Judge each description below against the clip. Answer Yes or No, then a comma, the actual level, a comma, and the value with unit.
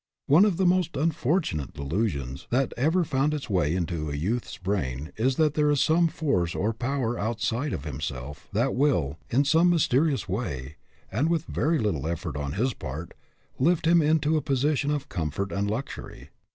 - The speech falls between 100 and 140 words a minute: No, average, 180 wpm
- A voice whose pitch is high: No, low, 120 Hz